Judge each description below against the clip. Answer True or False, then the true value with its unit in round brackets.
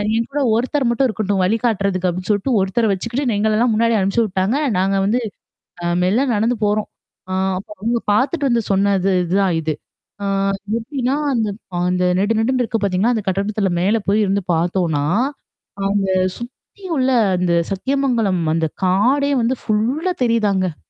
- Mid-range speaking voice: False (215 Hz)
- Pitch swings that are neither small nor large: True (3.9 semitones)